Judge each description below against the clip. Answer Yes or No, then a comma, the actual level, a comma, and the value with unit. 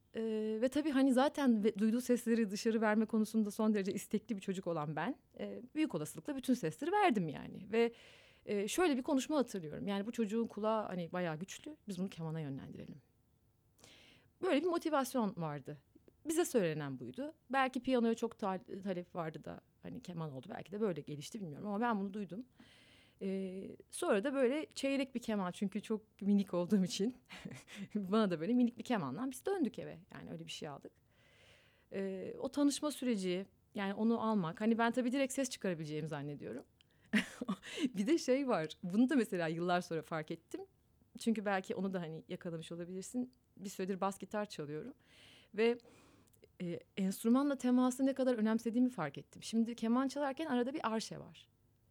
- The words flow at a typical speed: No, fast, 165 wpm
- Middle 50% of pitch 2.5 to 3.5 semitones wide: No, average, 5.1 semitones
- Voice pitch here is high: Yes, high, 220 Hz